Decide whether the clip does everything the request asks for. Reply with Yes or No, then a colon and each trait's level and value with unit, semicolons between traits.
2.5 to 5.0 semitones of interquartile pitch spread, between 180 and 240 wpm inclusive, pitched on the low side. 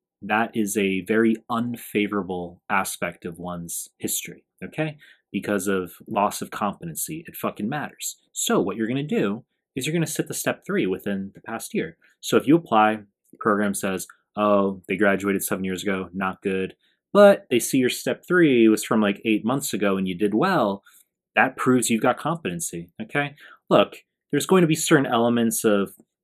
No: wide, 5.4 semitones; average, 185 wpm; low, 110 Hz